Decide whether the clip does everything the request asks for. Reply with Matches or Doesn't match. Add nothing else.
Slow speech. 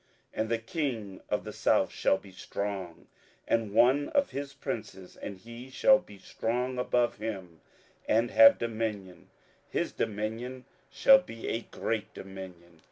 Doesn't match